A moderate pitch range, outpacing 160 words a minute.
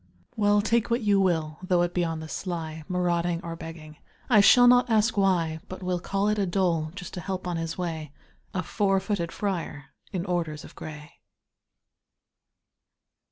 Yes: average, 3.4 semitones; average, 175 wpm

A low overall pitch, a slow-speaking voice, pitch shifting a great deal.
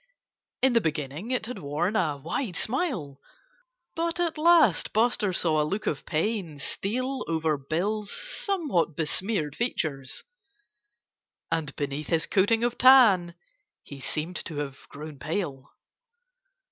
No: medium, 175 Hz; slow, 130 wpm; wide, 7.7 semitones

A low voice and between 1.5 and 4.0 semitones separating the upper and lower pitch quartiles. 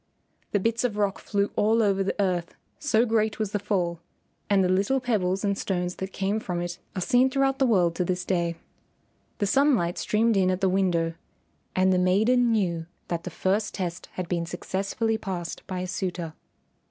No: high, 195 Hz; average, 3.3 semitones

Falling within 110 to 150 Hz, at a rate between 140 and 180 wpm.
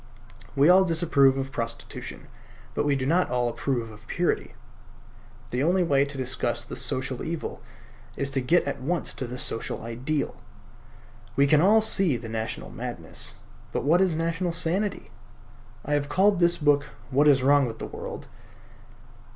Yes: medium, 140 Hz; average, 165 wpm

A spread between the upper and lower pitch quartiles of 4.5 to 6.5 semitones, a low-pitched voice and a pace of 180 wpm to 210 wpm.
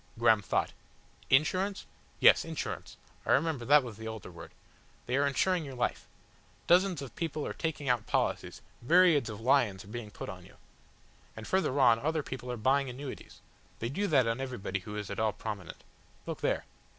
Yes: average, 5.2 semitones; low, 130 Hz; average, 185 wpm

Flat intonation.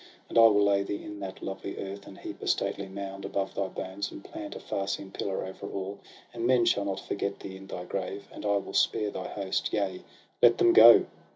Yes: narrow, 1.0 semitones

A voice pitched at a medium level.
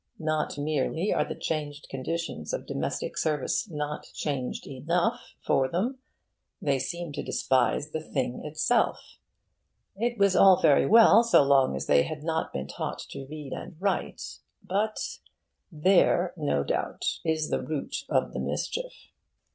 Yes: medium, 155 Hz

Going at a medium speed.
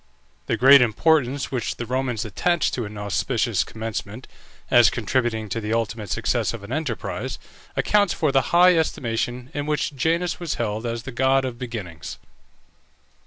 Yes: average, 160 wpm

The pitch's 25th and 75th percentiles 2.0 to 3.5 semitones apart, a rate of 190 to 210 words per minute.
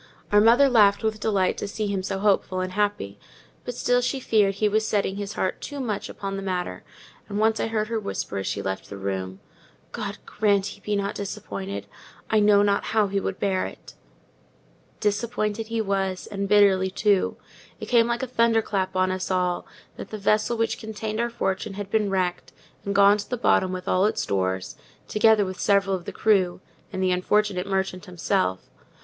Yes: narrow, 2.4 semitones; average, 200 wpm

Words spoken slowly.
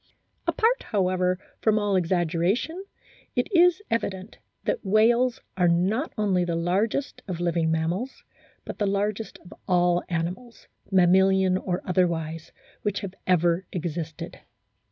Yes: slow, 130 wpm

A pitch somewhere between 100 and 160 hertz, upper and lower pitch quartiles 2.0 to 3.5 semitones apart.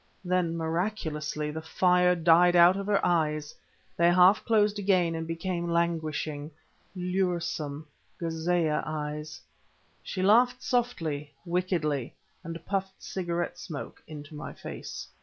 No: medium, 170 Hz; average, 2.8 semitones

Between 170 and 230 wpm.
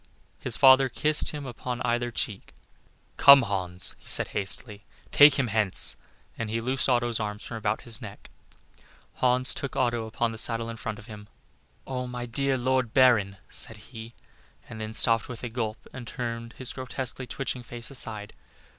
Yes: average, 175 wpm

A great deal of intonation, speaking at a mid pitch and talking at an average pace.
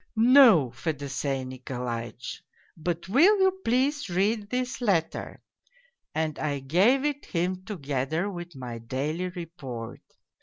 No: wide, 8.7 semitones; medium, 170 Hz; slow, 125 wpm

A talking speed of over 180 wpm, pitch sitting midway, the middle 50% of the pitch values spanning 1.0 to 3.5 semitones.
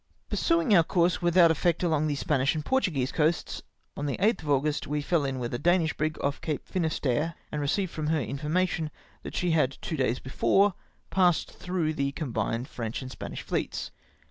No: average, 195 wpm; medium, 155 Hz; average, 3.9 semitones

